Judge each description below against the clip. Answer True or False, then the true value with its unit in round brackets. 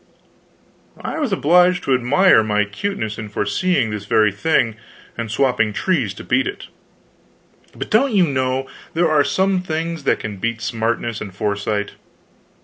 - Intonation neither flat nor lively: False (8.4 semitones)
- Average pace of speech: True (150 wpm)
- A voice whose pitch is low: True (125 Hz)